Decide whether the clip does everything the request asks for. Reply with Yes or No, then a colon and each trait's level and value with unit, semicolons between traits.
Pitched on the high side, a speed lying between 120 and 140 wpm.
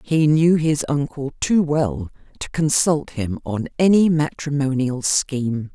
No: medium, 145 Hz; slow, 135 wpm